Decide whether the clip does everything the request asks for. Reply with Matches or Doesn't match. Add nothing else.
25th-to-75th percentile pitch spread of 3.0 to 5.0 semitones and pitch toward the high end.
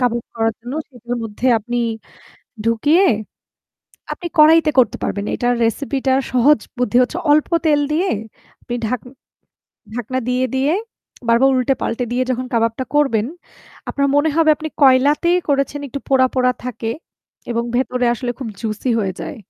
Matches